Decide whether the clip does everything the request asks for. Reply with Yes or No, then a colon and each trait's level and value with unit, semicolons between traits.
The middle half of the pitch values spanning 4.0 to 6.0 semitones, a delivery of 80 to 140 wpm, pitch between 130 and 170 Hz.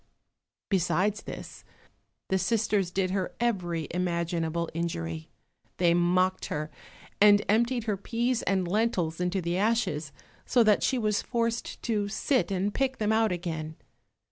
No: average, 4.3 semitones; slow, 135 wpm; high, 190 Hz